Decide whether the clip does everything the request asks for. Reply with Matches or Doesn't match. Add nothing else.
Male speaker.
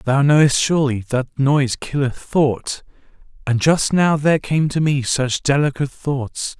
Matches